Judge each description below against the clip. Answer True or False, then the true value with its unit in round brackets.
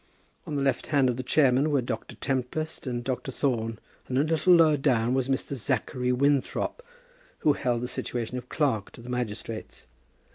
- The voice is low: True (130 Hz)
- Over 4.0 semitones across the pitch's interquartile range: False (2.6 semitones)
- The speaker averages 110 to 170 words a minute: False (180 wpm)